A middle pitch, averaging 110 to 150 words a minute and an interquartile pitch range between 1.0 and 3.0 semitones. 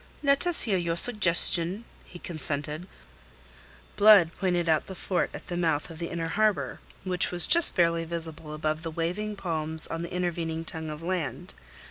No: medium, 170 Hz; average, 170 wpm; narrow, 2.4 semitones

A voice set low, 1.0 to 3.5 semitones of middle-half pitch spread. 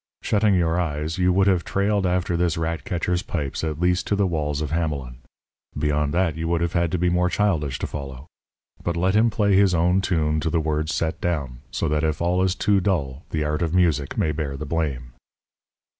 Yes: very low, 85 Hz; average, 3.1 semitones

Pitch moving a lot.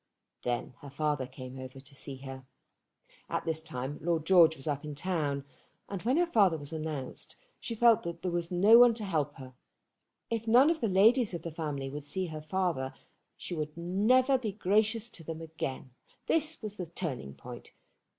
Yes: wide, 6.6 semitones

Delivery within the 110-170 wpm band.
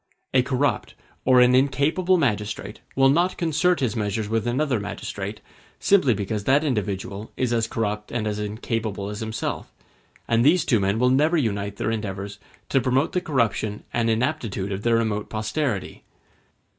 Yes: average, 160 wpm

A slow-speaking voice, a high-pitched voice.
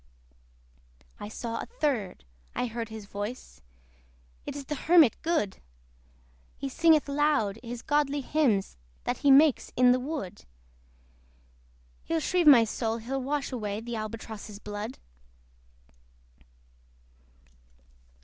Yes: slow, 115 wpm; very high, 250 Hz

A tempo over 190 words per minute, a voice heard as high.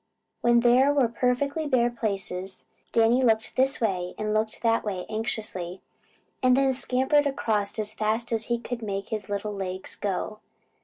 No: average, 160 wpm; high, 225 Hz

